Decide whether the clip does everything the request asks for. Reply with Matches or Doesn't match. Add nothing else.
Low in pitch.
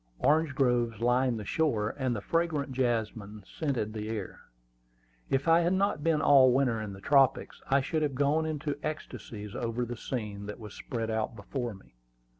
Matches